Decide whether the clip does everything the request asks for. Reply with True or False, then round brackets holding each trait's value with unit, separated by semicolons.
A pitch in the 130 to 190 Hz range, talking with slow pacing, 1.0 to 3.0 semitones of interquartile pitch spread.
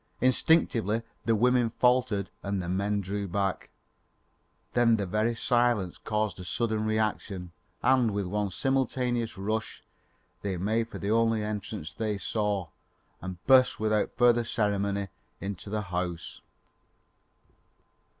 False (105 Hz; 125 wpm; 2.7 semitones)